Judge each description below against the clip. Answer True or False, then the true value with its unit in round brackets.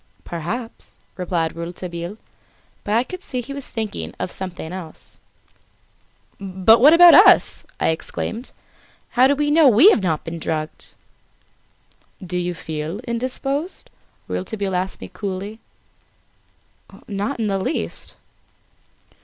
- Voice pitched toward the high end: True (195 Hz)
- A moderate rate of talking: False (130 wpm)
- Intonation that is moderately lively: False (6.2 semitones)